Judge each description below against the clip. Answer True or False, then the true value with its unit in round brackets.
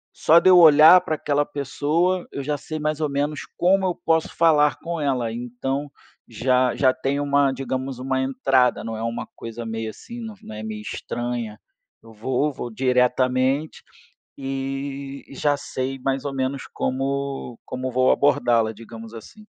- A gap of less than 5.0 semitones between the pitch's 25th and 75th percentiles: True (3.0 semitones)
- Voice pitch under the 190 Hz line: True (135 Hz)